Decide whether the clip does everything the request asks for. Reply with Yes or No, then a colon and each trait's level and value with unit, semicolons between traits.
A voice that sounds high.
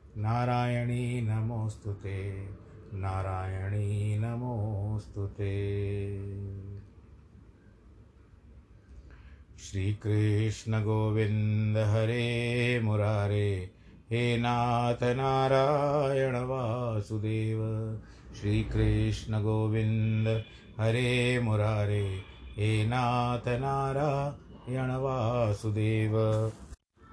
No: low, 110 Hz